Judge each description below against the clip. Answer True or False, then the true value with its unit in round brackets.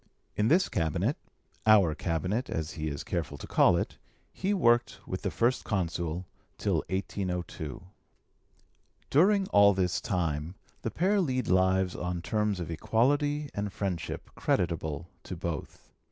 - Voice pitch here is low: True (95 Hz)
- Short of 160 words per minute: True (140 wpm)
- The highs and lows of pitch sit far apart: True (5.9 semitones)